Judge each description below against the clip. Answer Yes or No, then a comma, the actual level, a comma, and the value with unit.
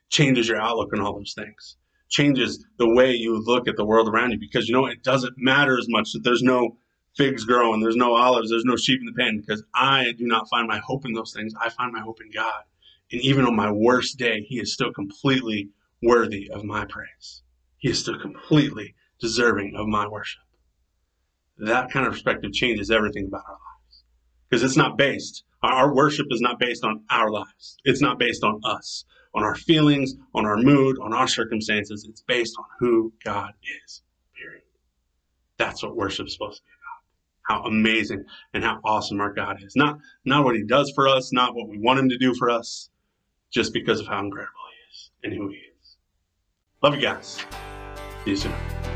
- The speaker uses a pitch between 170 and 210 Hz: No, low, 115 Hz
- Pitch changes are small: No, average, 3.4 semitones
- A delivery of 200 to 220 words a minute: Yes, fast, 205 wpm